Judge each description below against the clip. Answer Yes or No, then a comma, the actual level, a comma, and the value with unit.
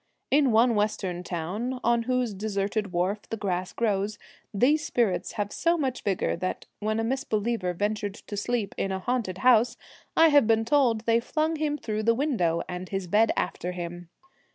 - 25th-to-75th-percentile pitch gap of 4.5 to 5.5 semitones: No, average, 4.0 semitones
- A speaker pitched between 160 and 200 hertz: No, high, 215 Hz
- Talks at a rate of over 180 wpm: No, average, 175 wpm